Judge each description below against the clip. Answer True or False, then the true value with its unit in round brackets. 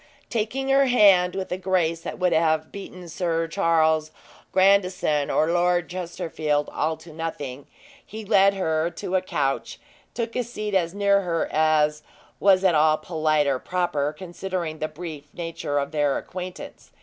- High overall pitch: False (170 Hz)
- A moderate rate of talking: True (160 wpm)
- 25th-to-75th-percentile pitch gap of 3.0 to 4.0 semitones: True (3.3 semitones)